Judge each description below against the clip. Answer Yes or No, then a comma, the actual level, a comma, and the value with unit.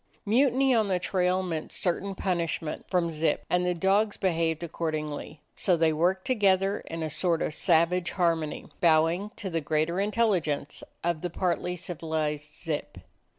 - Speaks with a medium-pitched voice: Yes, medium, 175 Hz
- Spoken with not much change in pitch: No, average, 3.0 semitones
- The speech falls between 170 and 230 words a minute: No, average, 160 wpm